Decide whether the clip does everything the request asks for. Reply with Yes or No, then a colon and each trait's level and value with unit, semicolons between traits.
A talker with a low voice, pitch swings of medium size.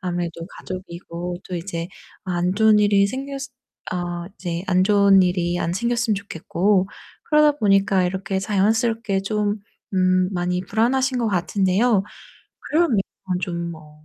No: high, 195 Hz; average, 3.5 semitones